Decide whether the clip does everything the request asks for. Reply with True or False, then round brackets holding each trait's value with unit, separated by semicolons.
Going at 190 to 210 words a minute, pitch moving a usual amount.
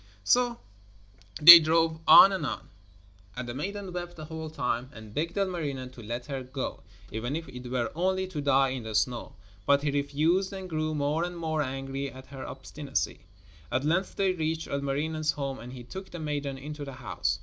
True (195 wpm; 4.1 semitones)